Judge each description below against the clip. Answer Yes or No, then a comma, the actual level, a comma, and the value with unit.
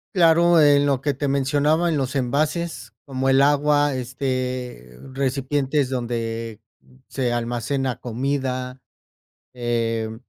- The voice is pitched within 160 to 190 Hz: No, low, 135 Hz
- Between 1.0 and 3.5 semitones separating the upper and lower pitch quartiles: Yes, average, 2.9 semitones